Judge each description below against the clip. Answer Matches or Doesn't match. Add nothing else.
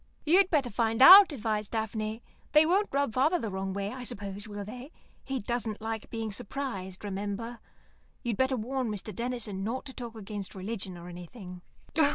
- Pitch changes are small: Doesn't match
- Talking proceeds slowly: Doesn't match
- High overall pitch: Matches